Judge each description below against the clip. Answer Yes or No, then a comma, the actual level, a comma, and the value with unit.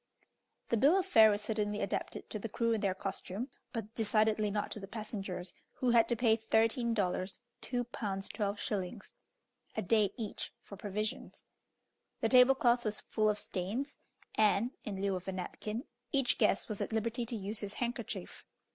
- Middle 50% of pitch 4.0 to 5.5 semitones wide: No, narrow, 2.6 semitones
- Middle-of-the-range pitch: No, high, 215 Hz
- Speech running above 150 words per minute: Yes, average, 175 wpm